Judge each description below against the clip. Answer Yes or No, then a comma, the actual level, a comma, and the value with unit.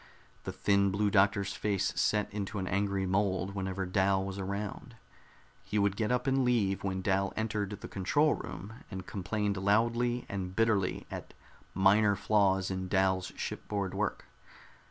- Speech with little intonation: Yes, narrow, 1.7 semitones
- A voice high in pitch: No, low, 100 Hz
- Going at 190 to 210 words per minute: No, average, 155 wpm